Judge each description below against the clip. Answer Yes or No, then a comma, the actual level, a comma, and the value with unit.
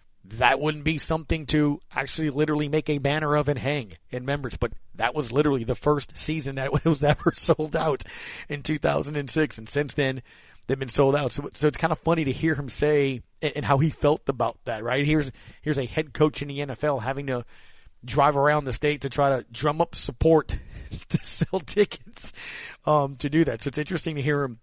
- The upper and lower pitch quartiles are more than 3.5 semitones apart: No, narrow, 2.5 semitones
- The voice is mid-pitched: Yes, medium, 145 Hz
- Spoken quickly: Yes, fast, 210 wpm